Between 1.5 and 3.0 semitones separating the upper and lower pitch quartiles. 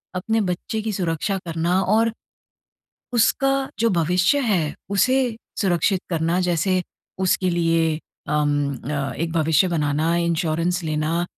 No: average, 3.4 semitones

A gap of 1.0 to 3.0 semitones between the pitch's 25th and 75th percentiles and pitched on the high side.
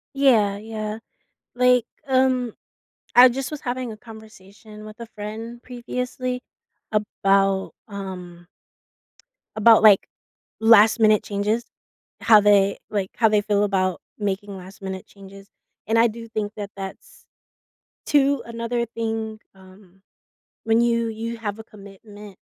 Yes: average, 2.7 semitones; high, 215 Hz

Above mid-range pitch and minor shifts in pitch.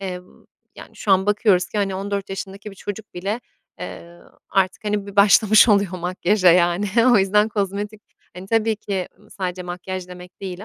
Yes: high, 195 Hz; narrow, 2.1 semitones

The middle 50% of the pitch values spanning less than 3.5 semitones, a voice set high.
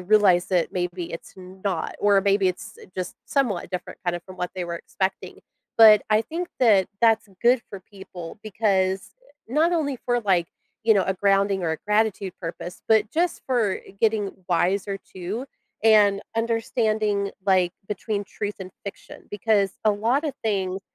Yes: average, 2.9 semitones; high, 200 Hz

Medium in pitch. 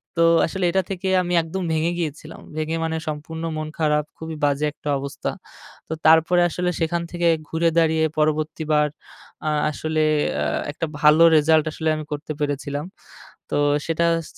Yes: medium, 160 Hz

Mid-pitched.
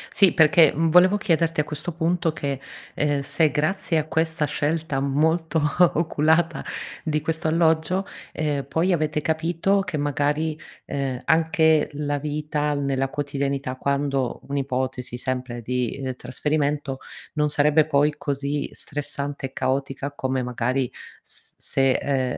Yes: medium, 150 Hz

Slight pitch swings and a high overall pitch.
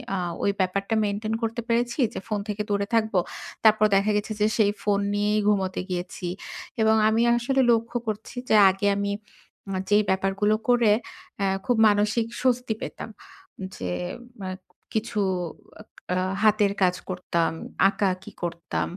Yes: narrow, 2.1 semitones; high, 210 Hz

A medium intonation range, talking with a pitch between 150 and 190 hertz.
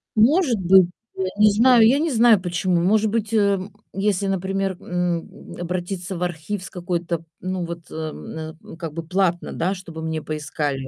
Yes: average, 3.2 semitones; medium, 185 Hz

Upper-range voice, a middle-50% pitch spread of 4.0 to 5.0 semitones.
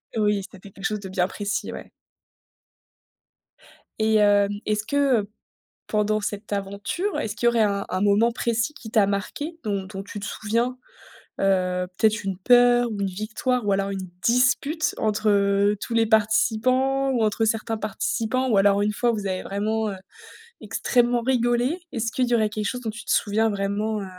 No: high, 215 Hz; average, 2.9 semitones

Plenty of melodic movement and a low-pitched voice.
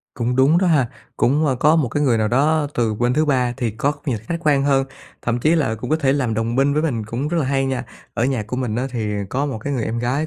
No: average, 3.6 semitones; low, 130 Hz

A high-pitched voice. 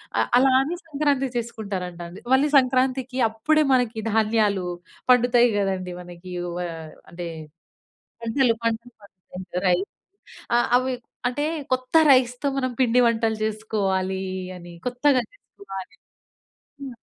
Yes: high, 230 Hz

